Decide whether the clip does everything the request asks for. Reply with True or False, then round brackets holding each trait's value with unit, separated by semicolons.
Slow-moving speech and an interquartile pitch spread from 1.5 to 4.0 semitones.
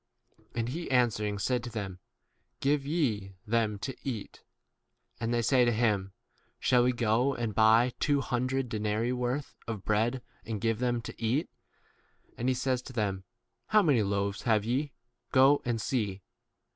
False (165 wpm; 3.2 semitones)